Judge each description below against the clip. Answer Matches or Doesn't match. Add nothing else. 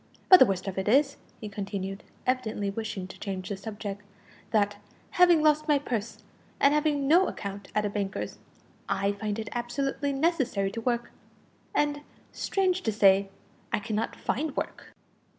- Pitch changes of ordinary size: Doesn't match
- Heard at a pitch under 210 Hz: Doesn't match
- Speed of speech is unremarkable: Matches